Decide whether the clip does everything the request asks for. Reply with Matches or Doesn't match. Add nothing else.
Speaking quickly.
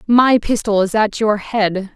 Doesn't match